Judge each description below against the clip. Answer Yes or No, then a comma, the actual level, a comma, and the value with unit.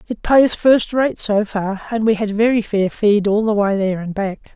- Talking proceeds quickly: Yes, fast, 235 wpm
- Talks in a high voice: Yes, high, 210 Hz